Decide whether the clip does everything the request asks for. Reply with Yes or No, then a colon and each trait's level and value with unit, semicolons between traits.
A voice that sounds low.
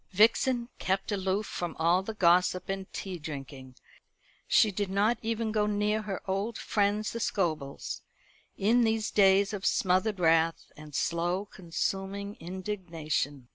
No: high, 195 Hz